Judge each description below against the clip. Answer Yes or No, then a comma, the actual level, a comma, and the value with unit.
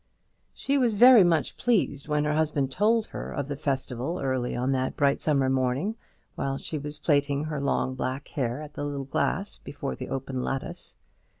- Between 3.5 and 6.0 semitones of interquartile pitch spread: No, average, 2.7 semitones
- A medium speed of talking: Yes, average, 185 wpm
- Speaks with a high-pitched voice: No, medium, 140 Hz